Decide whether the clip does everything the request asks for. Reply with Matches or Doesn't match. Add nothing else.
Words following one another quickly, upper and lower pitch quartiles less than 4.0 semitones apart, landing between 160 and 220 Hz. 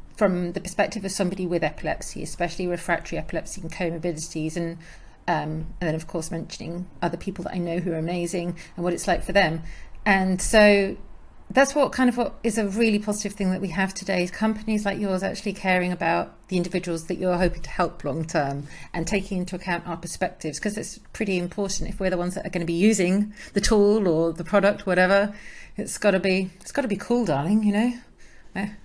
Matches